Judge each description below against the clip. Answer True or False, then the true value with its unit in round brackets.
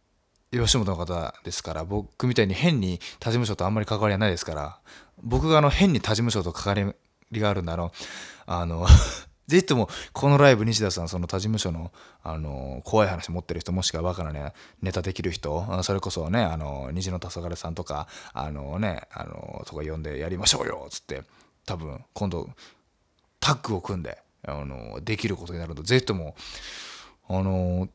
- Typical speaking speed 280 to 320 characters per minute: False (350 characters per minute)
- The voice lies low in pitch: True (90 Hz)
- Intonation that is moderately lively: True (4.8 semitones)